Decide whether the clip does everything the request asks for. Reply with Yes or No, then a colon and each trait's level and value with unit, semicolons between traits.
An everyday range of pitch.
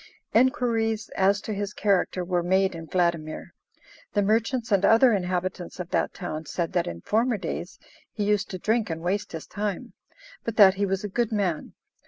Yes: average, 3.7 semitones